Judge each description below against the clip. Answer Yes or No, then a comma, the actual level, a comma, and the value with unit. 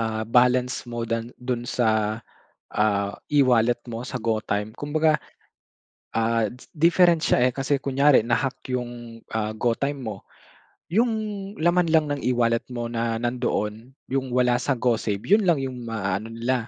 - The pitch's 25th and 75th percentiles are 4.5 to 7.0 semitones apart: No, average, 3.1 semitones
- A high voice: No, low, 120 Hz